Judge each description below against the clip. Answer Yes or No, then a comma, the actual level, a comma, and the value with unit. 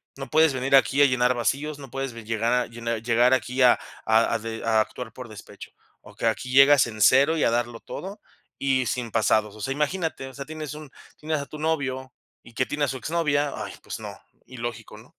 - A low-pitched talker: Yes, low, 130 Hz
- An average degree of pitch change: Yes, average, 3.6 semitones